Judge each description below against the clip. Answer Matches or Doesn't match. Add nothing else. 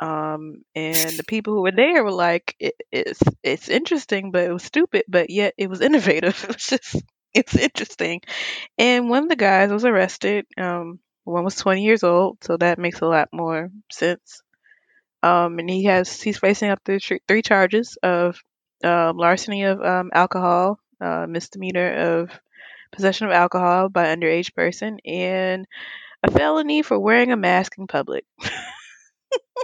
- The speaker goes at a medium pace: Matches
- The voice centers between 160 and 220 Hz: Matches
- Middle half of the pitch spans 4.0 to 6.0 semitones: Doesn't match